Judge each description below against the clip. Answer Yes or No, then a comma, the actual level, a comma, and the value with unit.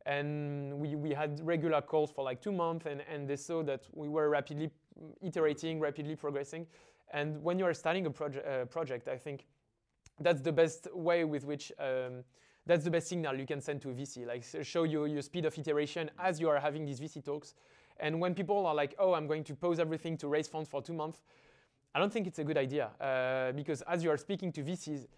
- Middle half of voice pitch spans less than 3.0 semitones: Yes, narrow, 2.4 semitones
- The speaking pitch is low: No, medium, 150 Hz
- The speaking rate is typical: No, fast, 230 wpm